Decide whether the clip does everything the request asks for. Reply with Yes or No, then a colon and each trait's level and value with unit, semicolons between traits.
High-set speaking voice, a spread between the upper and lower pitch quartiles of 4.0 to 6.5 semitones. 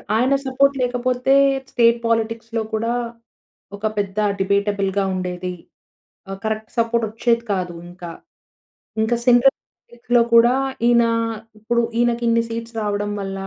No: high, 230 Hz; average, 2.9 semitones